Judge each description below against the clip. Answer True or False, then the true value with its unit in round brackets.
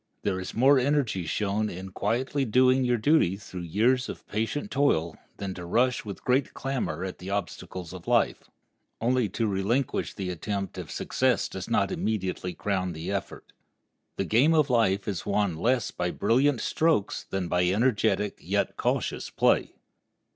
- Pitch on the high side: False (105 Hz)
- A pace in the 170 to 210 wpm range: False (160 wpm)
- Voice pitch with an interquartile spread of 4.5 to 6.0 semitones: True (5.4 semitones)